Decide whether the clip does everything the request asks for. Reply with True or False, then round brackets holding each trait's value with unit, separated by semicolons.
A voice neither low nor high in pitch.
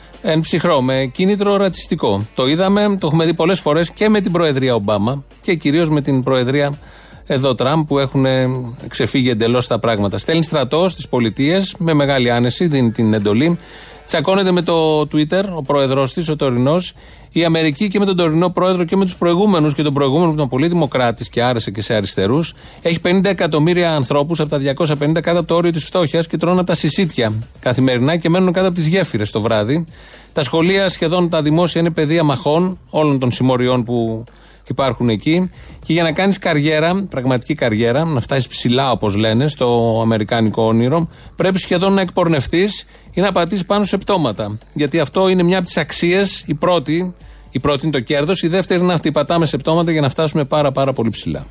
True (155 Hz)